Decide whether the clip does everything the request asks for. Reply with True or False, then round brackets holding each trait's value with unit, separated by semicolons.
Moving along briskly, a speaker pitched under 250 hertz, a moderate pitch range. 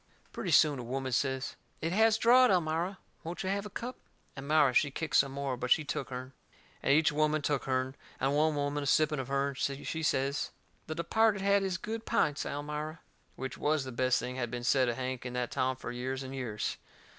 True (215 wpm; 140 Hz; 3.5 semitones)